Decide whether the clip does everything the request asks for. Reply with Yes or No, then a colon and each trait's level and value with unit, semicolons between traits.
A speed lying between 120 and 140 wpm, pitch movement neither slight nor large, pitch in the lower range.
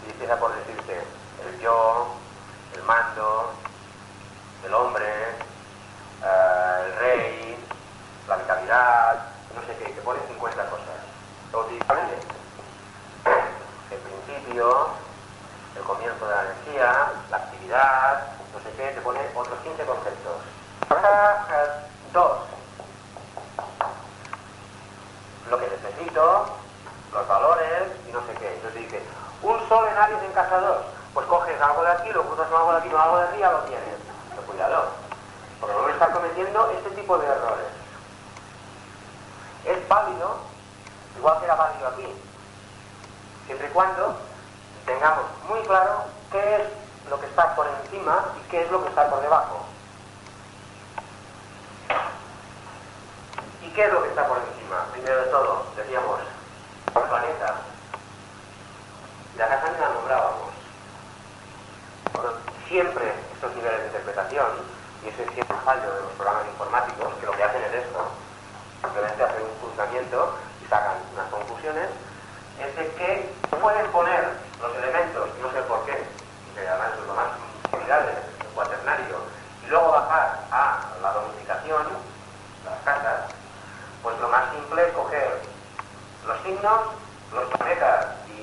No: average, 130 wpm; wide, 8.1 semitones; low, 110 Hz